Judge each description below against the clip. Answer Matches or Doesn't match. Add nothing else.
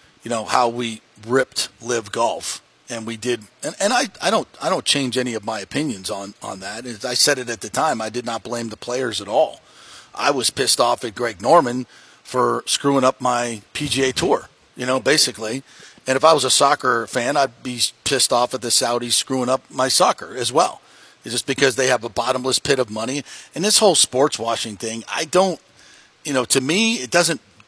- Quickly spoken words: Matches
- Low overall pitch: Matches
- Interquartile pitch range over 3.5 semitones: Doesn't match